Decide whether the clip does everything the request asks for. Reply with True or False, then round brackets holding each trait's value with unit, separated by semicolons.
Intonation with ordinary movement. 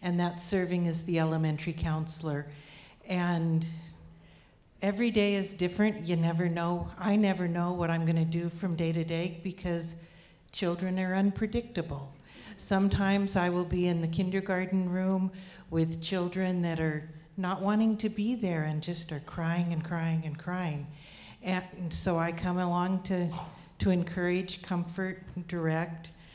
False (2.2 semitones)